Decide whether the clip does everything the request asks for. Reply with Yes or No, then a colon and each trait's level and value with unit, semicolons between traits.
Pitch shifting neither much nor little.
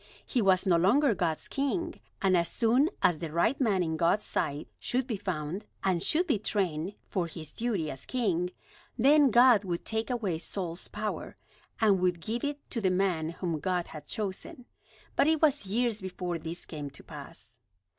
No: wide, 5.7 semitones